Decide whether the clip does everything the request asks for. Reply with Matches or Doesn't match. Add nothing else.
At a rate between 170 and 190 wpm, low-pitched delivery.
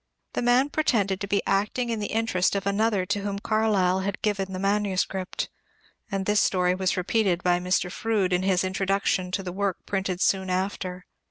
Doesn't match